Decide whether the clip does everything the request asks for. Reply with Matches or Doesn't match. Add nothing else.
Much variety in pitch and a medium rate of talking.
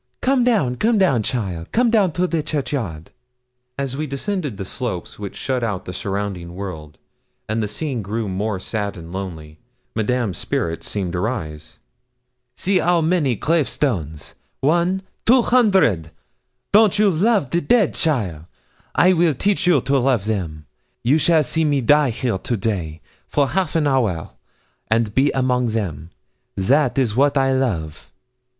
Matches